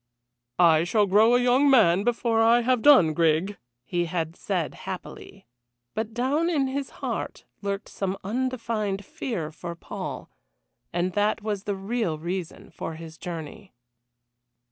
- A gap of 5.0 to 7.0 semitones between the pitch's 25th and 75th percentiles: Yes, wide, 5.6 semitones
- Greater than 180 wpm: No, average, 145 wpm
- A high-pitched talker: Yes, high, 200 Hz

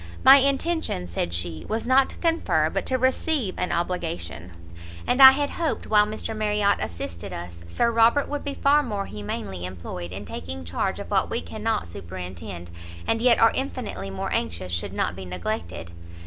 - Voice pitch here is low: No, medium, 160 Hz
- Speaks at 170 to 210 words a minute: Yes, average, 175 wpm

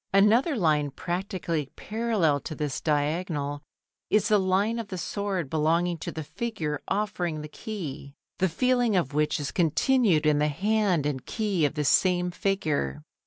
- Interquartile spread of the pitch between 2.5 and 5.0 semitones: No, wide, 5.4 semitones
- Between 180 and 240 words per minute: No, average, 160 wpm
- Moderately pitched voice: Yes, medium, 175 Hz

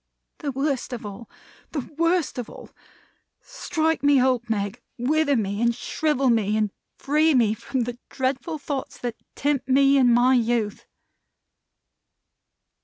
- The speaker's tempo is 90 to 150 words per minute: Yes, average, 140 wpm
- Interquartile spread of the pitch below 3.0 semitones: No, average, 3.5 semitones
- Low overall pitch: No, very high, 255 Hz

